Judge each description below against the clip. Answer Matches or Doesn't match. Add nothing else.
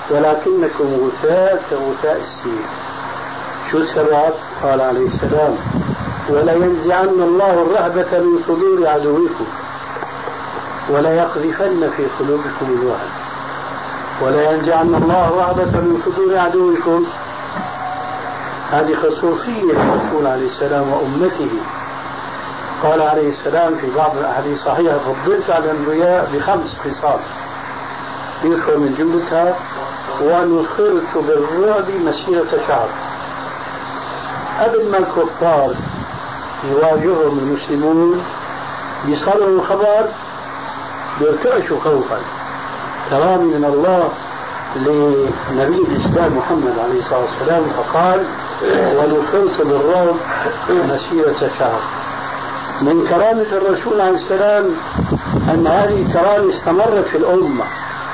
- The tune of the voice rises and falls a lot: Doesn't match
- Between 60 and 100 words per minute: Matches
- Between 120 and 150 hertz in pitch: Doesn't match